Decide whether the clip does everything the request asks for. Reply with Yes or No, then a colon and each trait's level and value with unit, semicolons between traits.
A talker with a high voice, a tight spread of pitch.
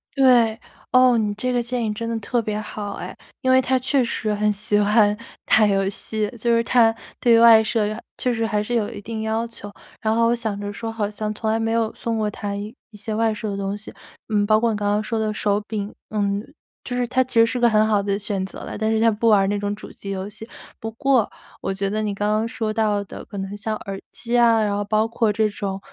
Yes: high, 215 Hz; narrow, 2.0 semitones